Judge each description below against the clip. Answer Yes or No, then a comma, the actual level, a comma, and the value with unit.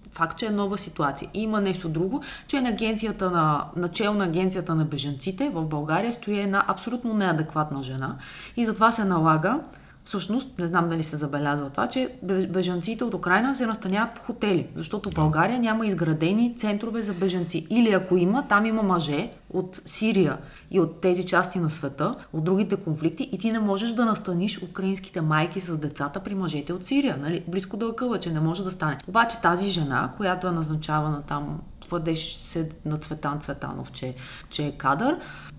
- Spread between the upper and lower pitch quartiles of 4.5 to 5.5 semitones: Yes, average, 4.9 semitones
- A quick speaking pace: Yes, fast, 180 wpm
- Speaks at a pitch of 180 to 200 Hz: Yes, medium, 185 Hz